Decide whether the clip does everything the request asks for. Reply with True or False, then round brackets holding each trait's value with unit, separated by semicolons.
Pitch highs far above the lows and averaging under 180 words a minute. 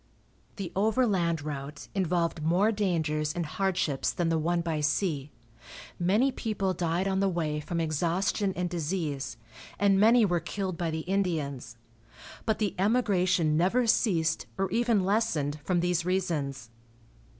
False (3.7 semitones; 140 wpm)